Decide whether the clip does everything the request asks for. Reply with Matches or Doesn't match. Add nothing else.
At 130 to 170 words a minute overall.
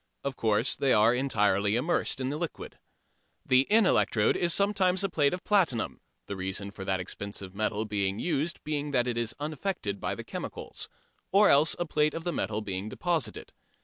Doesn't match